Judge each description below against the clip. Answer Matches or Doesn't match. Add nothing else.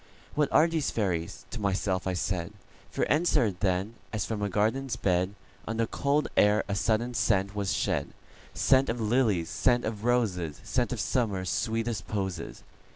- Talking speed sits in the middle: Matches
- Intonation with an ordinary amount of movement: Matches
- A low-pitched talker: Matches